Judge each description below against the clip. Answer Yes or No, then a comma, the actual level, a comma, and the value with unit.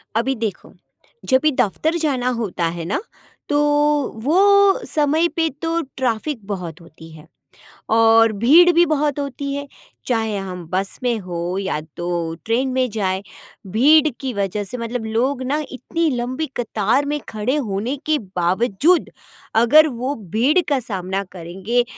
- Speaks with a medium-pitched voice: No, high, 240 Hz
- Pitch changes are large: Yes, wide, 6.6 semitones